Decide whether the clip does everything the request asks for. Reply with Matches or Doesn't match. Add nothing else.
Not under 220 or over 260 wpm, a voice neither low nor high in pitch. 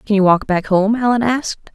Doesn't match